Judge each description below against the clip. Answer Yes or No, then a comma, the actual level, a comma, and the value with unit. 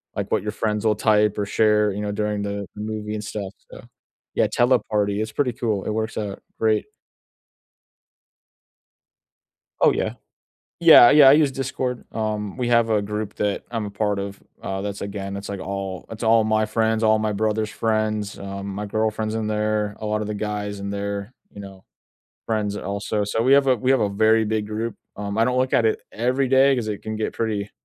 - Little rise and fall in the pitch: Yes, narrow, 1.6 semitones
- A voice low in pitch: Yes, low, 105 Hz